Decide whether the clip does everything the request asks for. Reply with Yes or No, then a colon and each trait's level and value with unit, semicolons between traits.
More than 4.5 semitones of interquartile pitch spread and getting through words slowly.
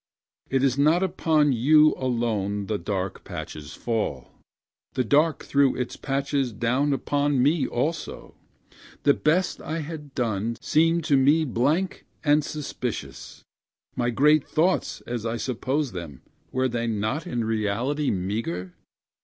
Yes: average, 4.9 semitones; slow, 130 wpm